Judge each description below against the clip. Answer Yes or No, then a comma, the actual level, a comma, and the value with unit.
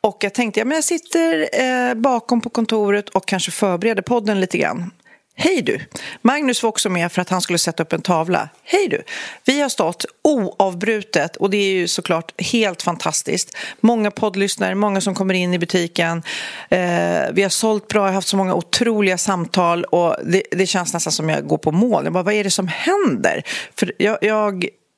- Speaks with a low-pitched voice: No, high, 200 Hz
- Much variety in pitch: No, average, 4.3 semitones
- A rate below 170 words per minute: No, fast, 195 wpm